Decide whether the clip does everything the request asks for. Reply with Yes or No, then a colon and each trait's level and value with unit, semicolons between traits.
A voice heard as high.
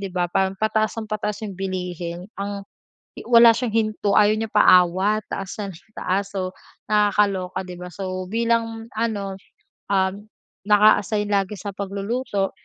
Yes: high, 200 Hz